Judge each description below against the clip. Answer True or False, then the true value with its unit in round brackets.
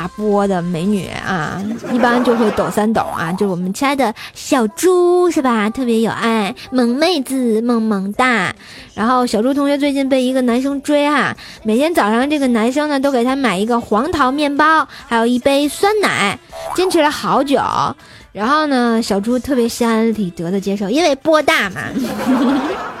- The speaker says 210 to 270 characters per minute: True (260 characters per minute)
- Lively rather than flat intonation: False (4.7 semitones)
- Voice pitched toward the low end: False (250 Hz)